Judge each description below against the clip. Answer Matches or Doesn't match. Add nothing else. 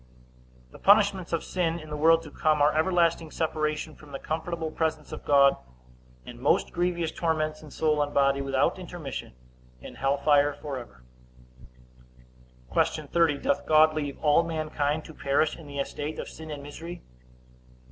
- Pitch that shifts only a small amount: Matches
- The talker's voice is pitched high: Doesn't match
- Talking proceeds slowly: Doesn't match